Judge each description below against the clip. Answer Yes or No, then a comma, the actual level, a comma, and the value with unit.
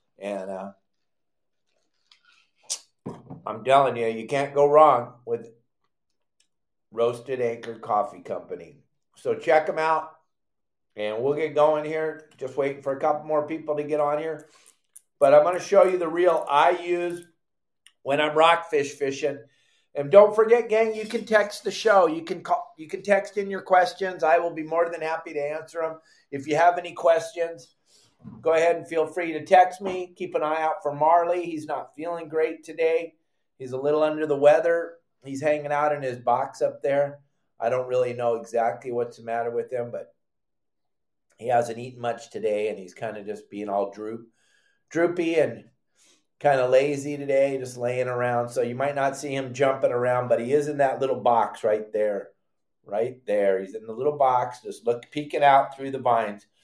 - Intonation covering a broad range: No, average, 5.0 semitones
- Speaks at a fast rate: No, average, 190 wpm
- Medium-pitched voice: Yes, medium, 150 Hz